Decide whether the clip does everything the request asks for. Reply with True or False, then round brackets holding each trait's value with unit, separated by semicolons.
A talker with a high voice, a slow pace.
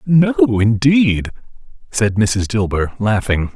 False (115 Hz; 100 wpm)